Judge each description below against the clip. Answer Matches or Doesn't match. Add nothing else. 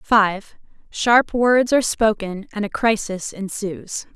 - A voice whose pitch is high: Matches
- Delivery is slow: Matches